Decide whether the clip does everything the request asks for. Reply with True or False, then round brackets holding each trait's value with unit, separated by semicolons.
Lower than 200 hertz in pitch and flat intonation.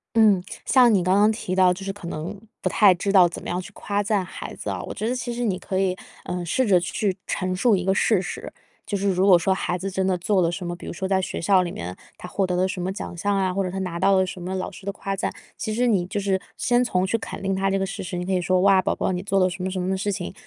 True (190 Hz; 1.7 semitones)